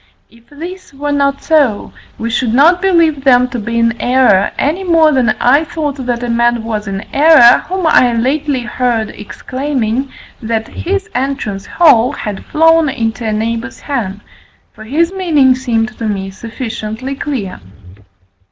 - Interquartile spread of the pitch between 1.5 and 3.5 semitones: No, average, 4.5 semitones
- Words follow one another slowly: No, average, 155 wpm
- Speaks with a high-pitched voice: Yes, very high, 255 Hz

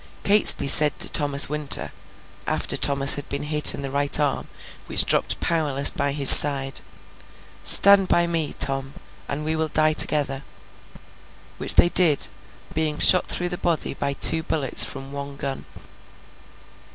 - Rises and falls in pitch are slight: Yes, narrow, 2.3 semitones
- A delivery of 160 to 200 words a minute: No, average, 150 wpm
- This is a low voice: No, medium, 145 Hz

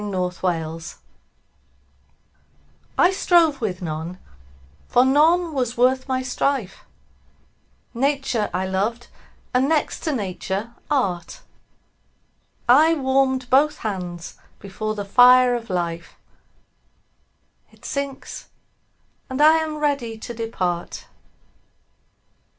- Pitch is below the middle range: No, high, 245 Hz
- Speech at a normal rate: No, slow, 100 wpm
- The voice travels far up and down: Yes, wide, 6.5 semitones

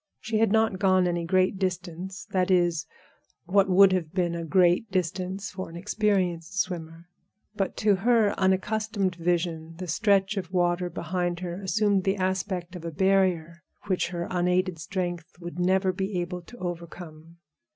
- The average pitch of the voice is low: No, medium, 185 Hz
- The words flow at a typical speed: Yes, average, 155 wpm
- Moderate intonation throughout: No, narrow, 1.9 semitones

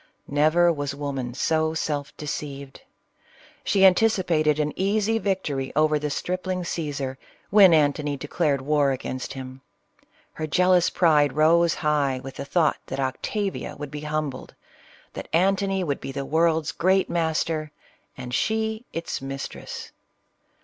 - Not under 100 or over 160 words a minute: Yes, average, 140 wpm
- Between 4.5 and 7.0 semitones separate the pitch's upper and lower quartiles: No, average, 4.1 semitones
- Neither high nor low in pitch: Yes, medium, 155 Hz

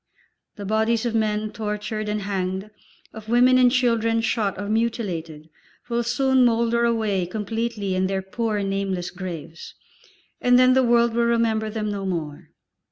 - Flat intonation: No, average, 3.2 semitones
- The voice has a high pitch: Yes, high, 220 Hz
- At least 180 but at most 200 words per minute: No, average, 155 wpm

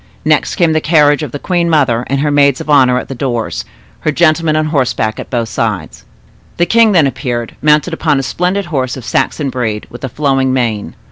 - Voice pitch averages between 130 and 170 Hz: Yes, medium, 140 Hz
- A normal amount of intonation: Yes, average, 3.7 semitones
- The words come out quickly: Yes, fast, 210 wpm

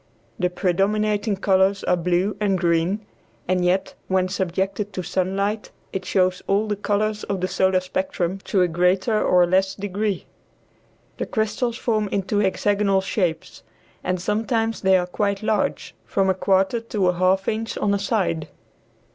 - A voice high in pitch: Yes, high, 195 Hz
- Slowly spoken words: No, average, 155 wpm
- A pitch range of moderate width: No, narrow, 2.3 semitones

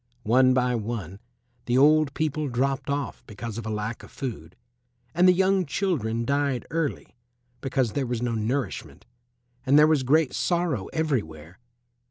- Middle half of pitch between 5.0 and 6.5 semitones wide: No, average, 4.6 semitones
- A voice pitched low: Yes, low, 130 Hz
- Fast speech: No, average, 155 wpm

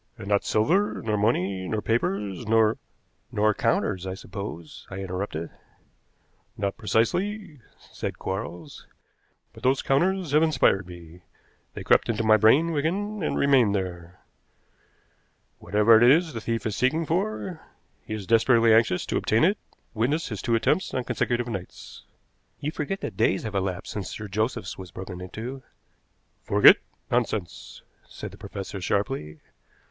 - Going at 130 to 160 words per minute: Yes, average, 150 wpm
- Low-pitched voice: Yes, low, 110 Hz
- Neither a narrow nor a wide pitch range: No, wide, 5.8 semitones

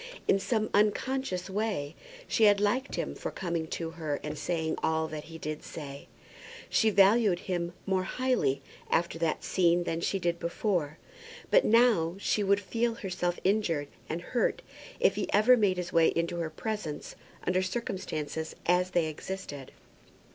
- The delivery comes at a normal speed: Yes, average, 160 wpm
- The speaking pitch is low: No, medium, 180 Hz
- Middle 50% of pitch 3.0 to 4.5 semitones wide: Yes, average, 4.1 semitones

